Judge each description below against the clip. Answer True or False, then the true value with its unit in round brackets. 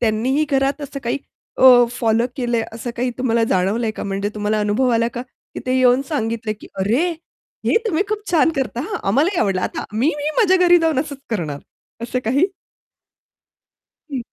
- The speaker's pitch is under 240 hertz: False (245 Hz)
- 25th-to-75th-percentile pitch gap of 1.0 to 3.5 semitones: False (4.6 semitones)